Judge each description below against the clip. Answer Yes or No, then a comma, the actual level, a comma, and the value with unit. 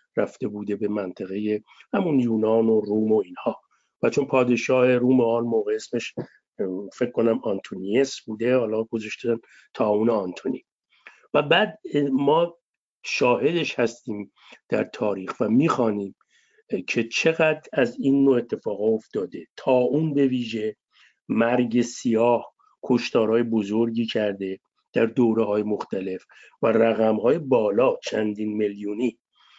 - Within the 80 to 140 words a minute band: Yes, average, 125 wpm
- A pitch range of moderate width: Yes, average, 3.6 semitones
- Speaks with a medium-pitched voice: No, low, 115 Hz